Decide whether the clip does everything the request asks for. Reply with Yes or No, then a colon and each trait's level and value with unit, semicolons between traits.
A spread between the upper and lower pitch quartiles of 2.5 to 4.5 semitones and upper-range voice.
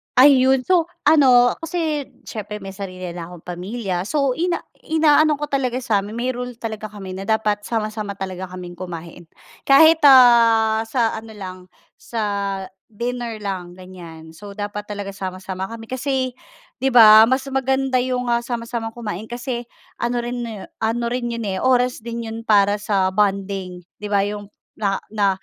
Yes: average, 4.1 semitones; high, 220 Hz